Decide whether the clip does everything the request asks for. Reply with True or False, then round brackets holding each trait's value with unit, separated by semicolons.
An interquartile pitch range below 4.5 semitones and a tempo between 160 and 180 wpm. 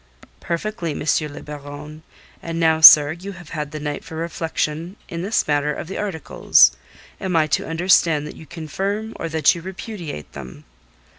True (2.8 semitones; 170 wpm)